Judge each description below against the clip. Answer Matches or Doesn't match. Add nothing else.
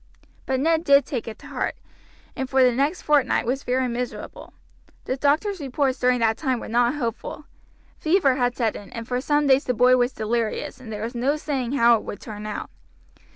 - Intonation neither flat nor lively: Matches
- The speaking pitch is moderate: Doesn't match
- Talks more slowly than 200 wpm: Doesn't match